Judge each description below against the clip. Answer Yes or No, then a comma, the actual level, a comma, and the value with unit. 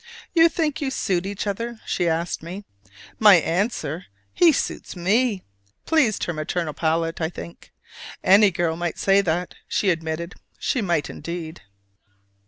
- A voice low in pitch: No, medium, 180 Hz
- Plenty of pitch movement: No, average, 4.3 semitones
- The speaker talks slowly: No, average, 145 wpm